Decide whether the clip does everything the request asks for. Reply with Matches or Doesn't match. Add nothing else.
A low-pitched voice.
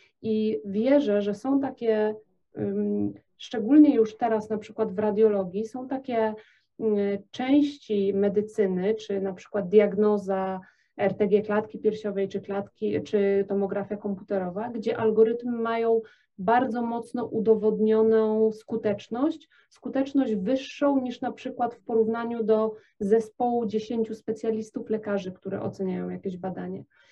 Doesn't match